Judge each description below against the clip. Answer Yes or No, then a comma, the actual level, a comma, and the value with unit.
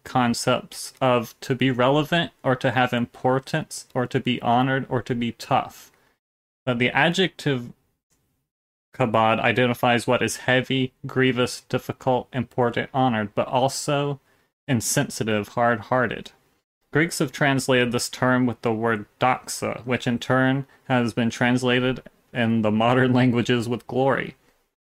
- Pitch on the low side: Yes, low, 125 Hz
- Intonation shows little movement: Yes, narrow, 1.6 semitones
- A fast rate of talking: No, average, 135 wpm